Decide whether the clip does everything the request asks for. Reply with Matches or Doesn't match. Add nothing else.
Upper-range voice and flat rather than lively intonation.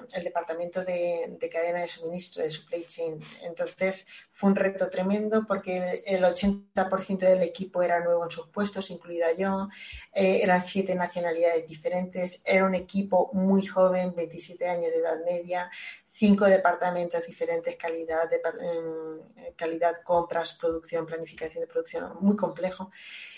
Doesn't match